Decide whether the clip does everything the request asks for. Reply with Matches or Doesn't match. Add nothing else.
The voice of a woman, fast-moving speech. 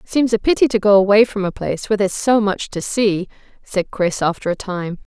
Matches